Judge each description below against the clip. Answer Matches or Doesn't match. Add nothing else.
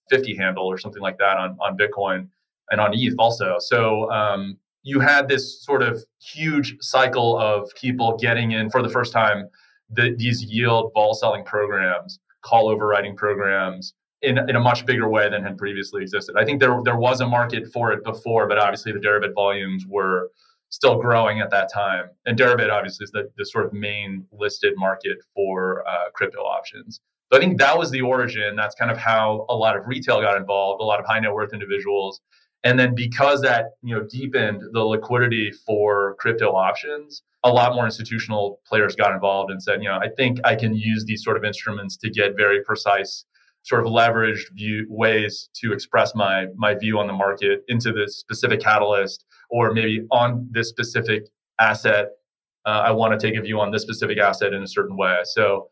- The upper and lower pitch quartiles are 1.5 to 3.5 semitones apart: Matches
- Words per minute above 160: Matches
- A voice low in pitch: Matches